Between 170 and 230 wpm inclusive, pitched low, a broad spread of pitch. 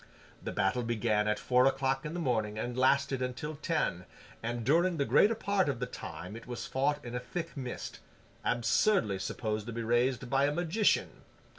No: average, 180 wpm; low, 125 Hz; average, 4.2 semitones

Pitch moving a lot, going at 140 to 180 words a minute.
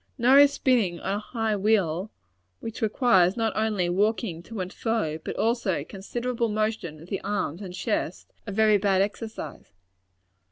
No: average, 3.4 semitones; average, 160 wpm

